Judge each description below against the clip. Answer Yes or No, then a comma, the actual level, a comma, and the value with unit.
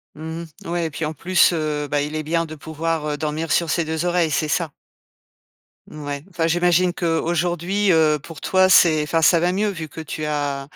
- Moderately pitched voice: Yes, medium, 160 Hz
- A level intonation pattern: Yes, narrow, 2.2 semitones